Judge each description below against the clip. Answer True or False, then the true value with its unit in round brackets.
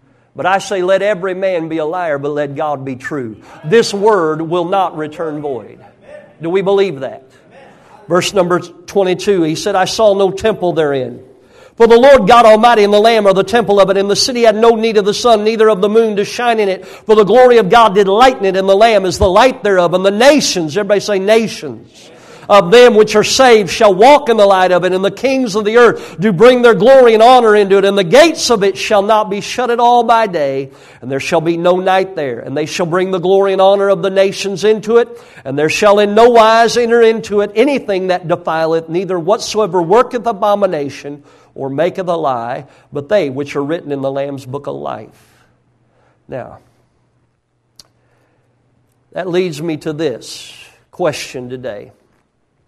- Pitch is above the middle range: True (195 Hz)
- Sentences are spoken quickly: True (210 wpm)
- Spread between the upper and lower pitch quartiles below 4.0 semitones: False (5.0 semitones)